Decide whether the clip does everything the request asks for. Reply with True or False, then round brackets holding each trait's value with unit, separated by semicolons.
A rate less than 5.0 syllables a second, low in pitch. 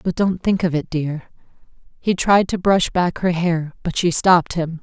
False (4.5 syllables/s; 175 Hz)